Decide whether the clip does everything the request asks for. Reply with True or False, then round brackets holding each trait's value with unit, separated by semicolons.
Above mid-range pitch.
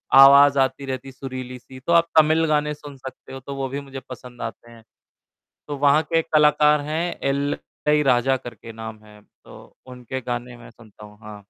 False (135 Hz)